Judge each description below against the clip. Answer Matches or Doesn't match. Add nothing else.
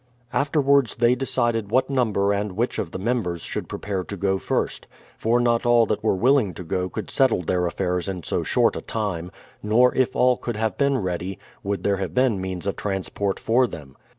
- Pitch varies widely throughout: Doesn't match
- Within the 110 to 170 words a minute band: Doesn't match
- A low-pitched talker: Matches